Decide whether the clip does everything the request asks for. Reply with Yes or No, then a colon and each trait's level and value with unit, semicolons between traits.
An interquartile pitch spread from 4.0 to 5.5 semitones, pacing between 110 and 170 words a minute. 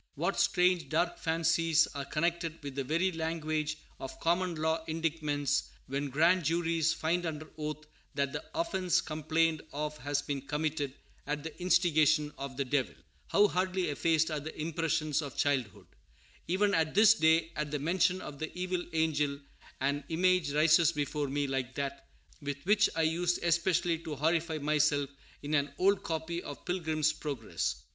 No: average, 2.7 semitones; average, 160 wpm